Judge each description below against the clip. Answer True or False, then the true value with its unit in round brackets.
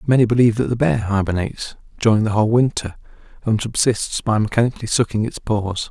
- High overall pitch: False (110 Hz)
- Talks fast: False (175 wpm)